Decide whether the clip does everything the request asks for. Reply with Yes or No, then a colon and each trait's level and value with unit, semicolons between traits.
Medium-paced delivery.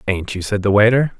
No: fast, 250 wpm